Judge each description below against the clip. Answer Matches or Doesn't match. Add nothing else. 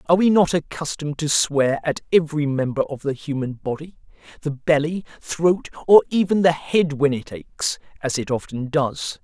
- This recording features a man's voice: Matches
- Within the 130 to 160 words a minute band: Doesn't match